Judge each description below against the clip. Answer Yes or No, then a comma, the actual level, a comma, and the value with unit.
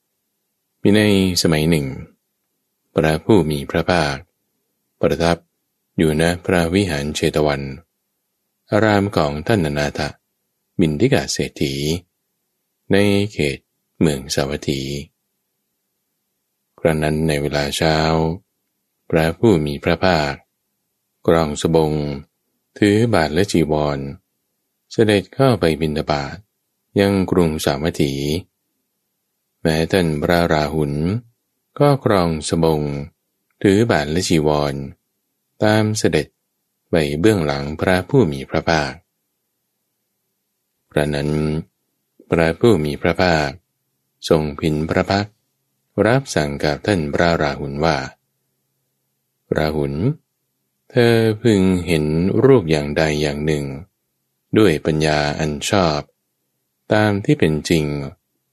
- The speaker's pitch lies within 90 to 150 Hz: No, very low, 80 Hz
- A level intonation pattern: No, average, 4.8 semitones